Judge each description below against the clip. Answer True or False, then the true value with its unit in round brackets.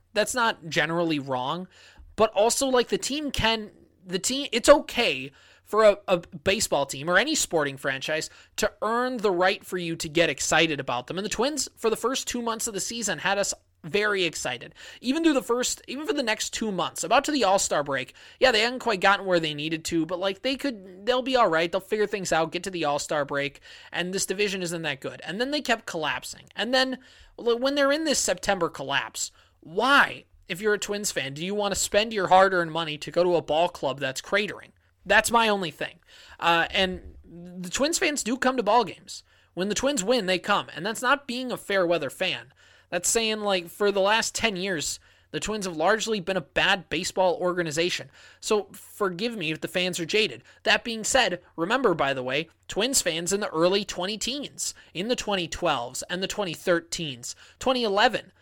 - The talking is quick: True (210 wpm)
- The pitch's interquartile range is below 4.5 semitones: False (5.2 semitones)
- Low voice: False (190 Hz)